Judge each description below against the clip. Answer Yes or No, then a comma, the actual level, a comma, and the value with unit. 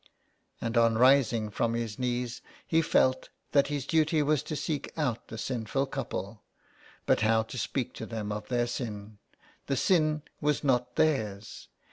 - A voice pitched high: No, low, 125 Hz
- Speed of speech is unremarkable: Yes, average, 160 wpm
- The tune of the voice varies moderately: Yes, average, 4.2 semitones